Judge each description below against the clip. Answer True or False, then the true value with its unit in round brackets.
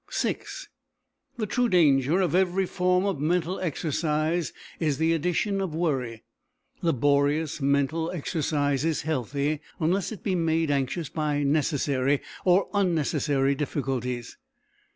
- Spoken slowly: True (120 wpm)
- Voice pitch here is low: False (155 Hz)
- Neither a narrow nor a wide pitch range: True (3.8 semitones)